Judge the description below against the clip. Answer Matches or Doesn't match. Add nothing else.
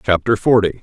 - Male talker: Matches